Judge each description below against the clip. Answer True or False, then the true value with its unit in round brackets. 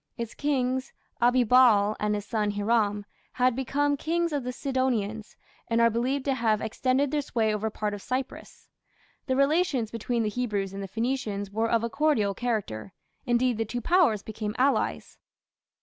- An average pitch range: True (3.7 semitones)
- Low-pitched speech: False (235 Hz)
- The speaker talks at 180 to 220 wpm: False (165 wpm)